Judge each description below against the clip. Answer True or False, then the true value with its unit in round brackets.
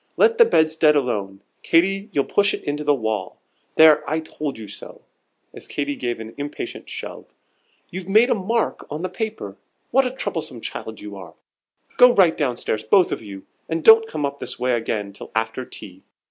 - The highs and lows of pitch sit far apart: True (9.0 semitones)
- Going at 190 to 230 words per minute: True (195 wpm)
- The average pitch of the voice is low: False (150 Hz)